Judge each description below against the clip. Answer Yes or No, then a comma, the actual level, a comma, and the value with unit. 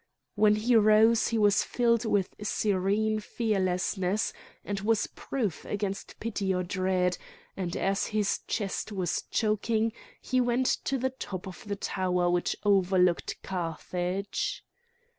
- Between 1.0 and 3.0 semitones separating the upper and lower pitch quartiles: Yes, average, 2.7 semitones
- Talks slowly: Yes, slow, 130 wpm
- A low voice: No, high, 205 Hz